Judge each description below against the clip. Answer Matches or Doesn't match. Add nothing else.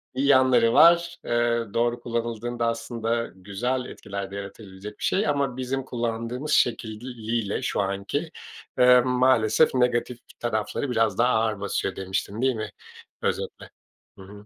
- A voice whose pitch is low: Matches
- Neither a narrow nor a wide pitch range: Matches